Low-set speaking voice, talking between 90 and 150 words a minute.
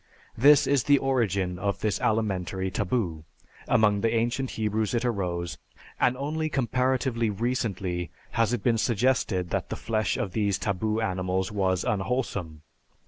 Yes: low, 110 Hz; average, 140 wpm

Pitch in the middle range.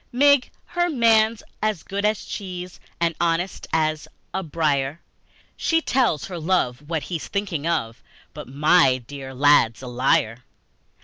Yes: medium, 165 Hz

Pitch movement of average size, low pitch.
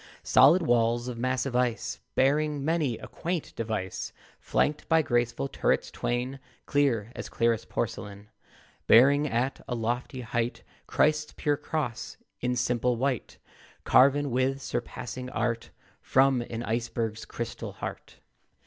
Yes: average, 3.0 semitones; low, 125 Hz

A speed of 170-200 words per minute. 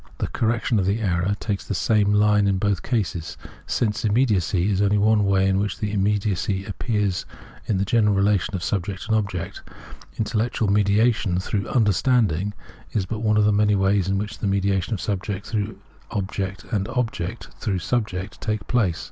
Yes: average, 180 wpm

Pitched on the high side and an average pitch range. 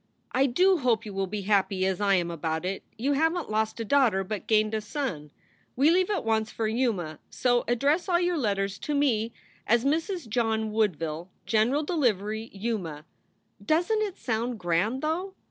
No: high, 225 Hz; wide, 6.2 semitones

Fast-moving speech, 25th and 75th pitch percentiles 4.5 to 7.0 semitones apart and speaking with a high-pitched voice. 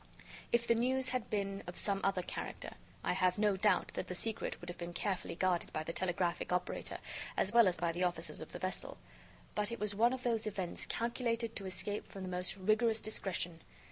No: fast, 210 wpm; average, 3.9 semitones; high, 195 Hz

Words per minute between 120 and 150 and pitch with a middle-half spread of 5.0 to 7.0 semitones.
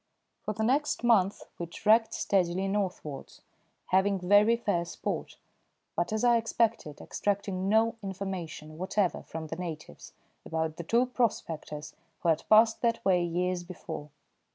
No: average, 140 wpm; average, 4.3 semitones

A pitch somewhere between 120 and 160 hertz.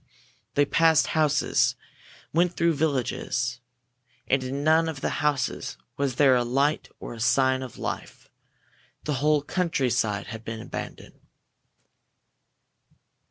Yes: medium, 140 Hz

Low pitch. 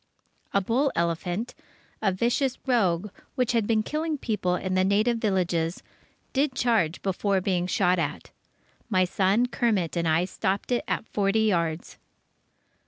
No: high, 195 Hz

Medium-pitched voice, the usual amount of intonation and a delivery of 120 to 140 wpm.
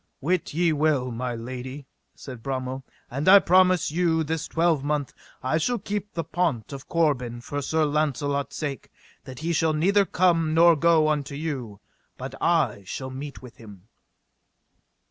No: medium, 150 Hz; average, 4.2 semitones; average, 155 wpm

